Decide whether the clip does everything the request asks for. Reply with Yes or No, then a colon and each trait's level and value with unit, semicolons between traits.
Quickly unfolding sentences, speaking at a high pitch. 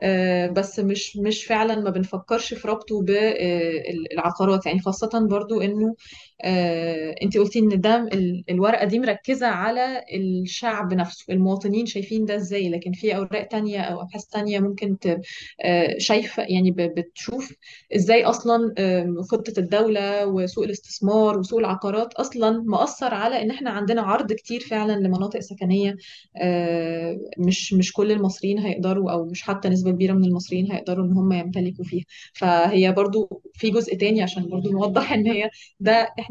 Yes: fast, 145 wpm; high, 200 Hz